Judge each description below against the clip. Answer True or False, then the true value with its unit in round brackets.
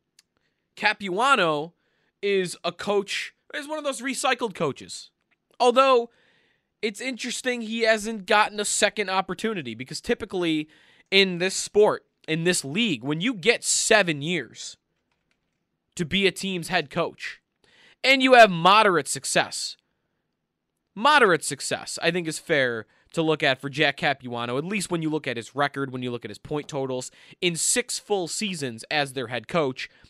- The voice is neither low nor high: True (180 Hz)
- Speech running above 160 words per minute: False (155 wpm)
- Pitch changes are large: True (7.3 semitones)